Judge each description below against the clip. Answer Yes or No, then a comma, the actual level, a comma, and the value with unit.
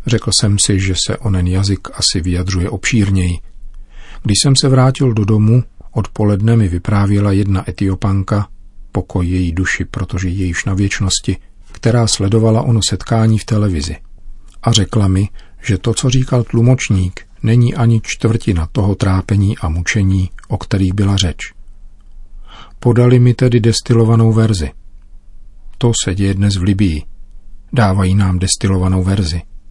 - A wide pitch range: No, average, 3.0 semitones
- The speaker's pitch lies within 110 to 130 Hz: No, low, 100 Hz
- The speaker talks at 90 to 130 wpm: No, average, 140 wpm